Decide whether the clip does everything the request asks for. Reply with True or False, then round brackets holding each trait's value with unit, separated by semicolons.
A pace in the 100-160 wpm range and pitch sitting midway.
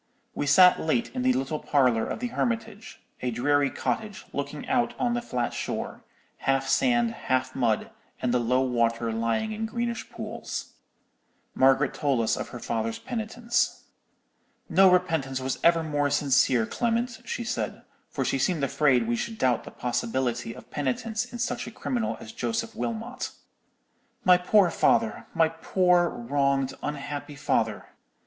True (155 wpm; 150 Hz)